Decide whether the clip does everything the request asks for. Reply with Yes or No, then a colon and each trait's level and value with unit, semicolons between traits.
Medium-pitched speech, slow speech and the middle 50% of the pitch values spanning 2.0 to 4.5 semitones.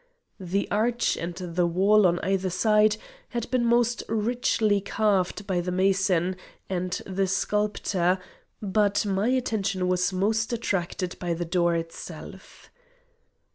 No: high, 195 Hz; slow, 130 wpm; average, 2.8 semitones